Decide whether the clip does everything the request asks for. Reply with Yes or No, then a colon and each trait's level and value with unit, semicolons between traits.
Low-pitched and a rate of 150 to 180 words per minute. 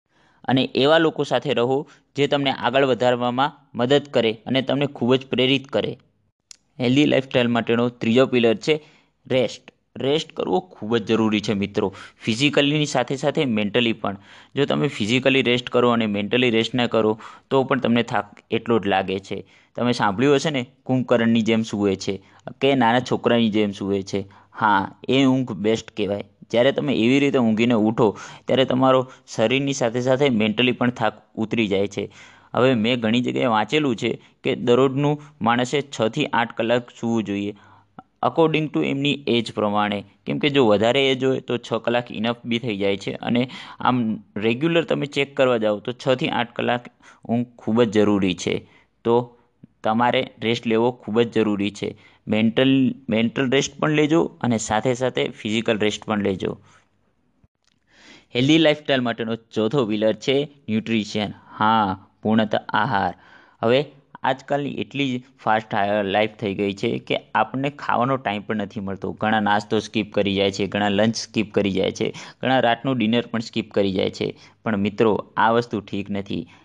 Yes: low, 115 Hz; fast, 165 wpm